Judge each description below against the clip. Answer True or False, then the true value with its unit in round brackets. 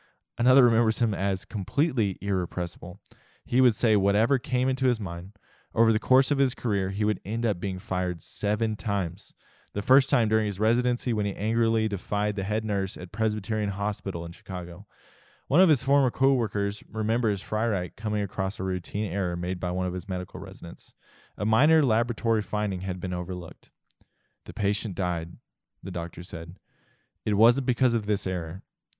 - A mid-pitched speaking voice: False (105 Hz)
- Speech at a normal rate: True (175 wpm)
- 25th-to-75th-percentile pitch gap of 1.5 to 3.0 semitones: False (3.8 semitones)